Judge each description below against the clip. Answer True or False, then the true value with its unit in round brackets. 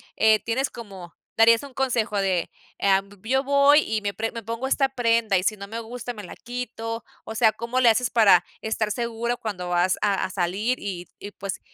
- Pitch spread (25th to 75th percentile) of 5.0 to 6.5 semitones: False (3.3 semitones)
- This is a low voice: False (225 Hz)